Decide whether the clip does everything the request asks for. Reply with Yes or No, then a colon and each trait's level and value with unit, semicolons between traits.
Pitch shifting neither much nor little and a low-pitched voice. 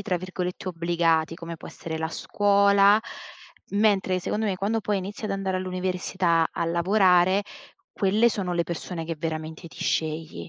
No: average, 3.0 semitones; medium, 185 Hz